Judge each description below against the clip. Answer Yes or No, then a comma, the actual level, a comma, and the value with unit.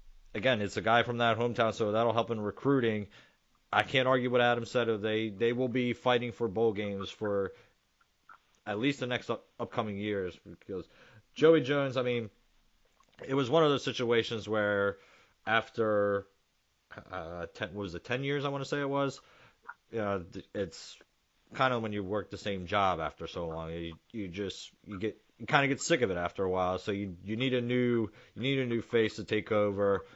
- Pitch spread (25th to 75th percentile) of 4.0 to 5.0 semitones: No, average, 3.6 semitones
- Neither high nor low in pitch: No, low, 115 Hz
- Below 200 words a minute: No, fast, 205 wpm